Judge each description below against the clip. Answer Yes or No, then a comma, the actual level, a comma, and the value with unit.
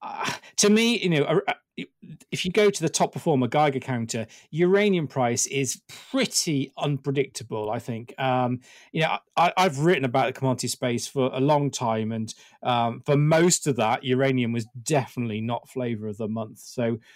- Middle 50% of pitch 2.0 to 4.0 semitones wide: No, average, 5.3 semitones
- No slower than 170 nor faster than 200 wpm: Yes, average, 180 wpm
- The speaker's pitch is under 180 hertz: Yes, low, 135 Hz